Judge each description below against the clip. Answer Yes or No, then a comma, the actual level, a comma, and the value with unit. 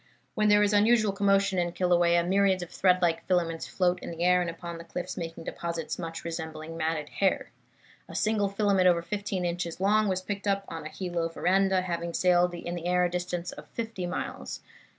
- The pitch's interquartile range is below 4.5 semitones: Yes, narrow, 2.5 semitones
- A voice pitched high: No, medium, 180 Hz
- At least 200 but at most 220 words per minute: Yes, fast, 205 wpm